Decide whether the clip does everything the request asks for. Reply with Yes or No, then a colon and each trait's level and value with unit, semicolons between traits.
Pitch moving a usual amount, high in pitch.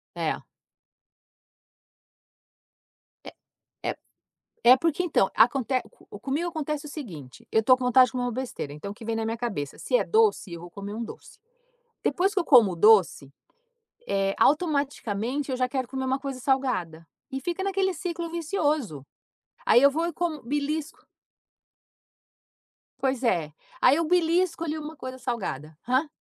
No: wide, 6.0 semitones; very high, 265 Hz